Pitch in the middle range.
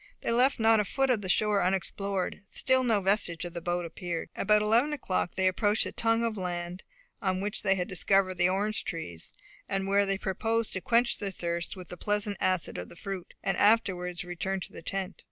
No: high, 195 Hz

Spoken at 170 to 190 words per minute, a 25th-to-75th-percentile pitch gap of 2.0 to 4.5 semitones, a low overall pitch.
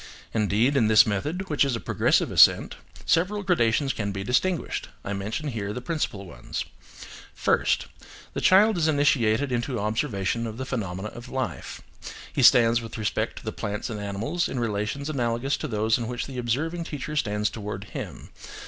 No: average, 175 wpm; average, 5.2 semitones; low, 120 Hz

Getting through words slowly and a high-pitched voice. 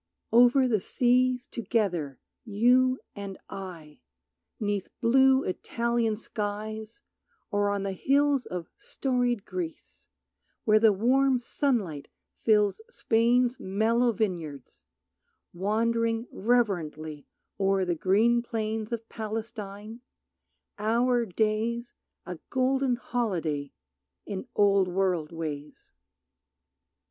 Yes: slow, 95 wpm; high, 220 Hz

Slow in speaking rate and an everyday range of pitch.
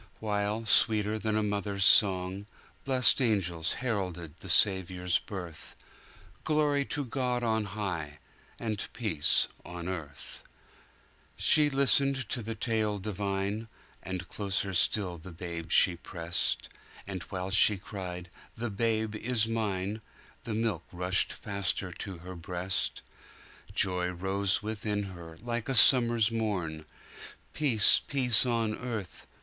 Yes: slow, 110 wpm; average, 3.7 semitones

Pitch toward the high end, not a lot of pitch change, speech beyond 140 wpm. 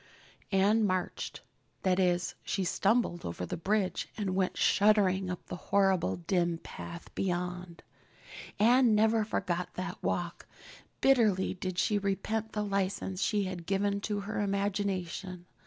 No: high, 195 Hz; narrow, 2.3 semitones; slow, 135 wpm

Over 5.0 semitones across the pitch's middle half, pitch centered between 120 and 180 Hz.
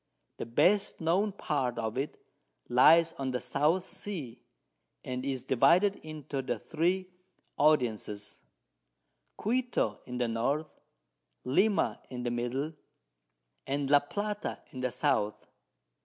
Yes: wide, 5.5 semitones; medium, 140 Hz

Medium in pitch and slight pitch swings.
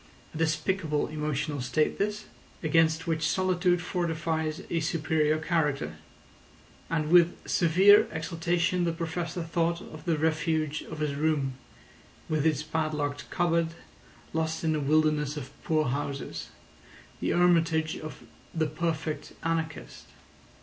Yes: medium, 160 Hz; narrow, 1.6 semitones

